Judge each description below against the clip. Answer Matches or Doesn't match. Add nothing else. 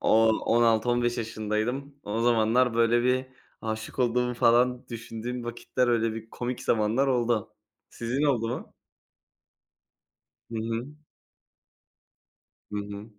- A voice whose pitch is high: Doesn't match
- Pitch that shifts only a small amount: Matches